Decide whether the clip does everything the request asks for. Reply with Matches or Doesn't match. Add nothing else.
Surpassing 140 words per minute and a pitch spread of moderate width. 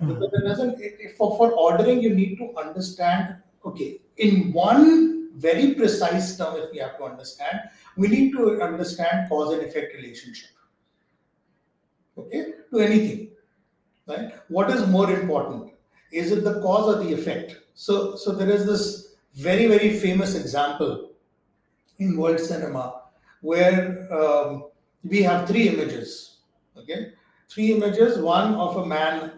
Doesn't match